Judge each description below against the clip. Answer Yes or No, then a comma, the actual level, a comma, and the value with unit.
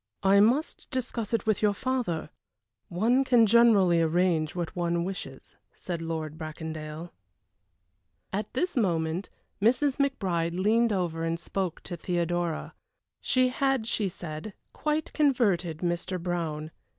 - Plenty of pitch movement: Yes, wide, 5.7 semitones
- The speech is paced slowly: Yes, slow, 125 wpm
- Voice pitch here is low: No, medium, 180 Hz